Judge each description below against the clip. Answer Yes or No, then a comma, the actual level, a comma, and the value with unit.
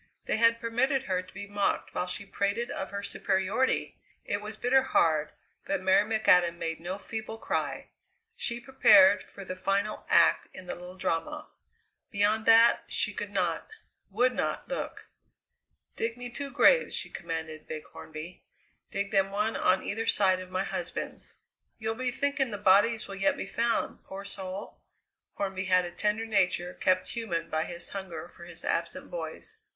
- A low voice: No, high, 200 Hz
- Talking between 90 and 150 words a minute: No, average, 170 wpm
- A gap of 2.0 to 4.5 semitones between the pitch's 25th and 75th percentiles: Yes, average, 3.7 semitones